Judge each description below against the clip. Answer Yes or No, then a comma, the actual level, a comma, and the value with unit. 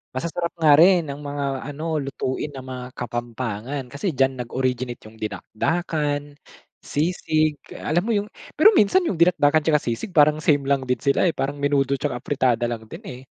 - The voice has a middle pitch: Yes, medium, 145 Hz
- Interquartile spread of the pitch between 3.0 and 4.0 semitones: Yes, average, 3.5 semitones